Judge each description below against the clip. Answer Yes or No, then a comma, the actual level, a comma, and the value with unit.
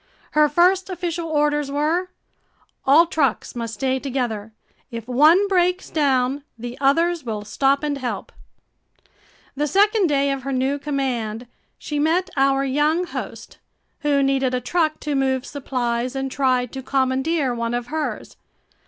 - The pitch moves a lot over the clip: No, average, 3.4 semitones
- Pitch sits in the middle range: No, very high, 275 Hz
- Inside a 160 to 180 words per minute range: No, average, 145 wpm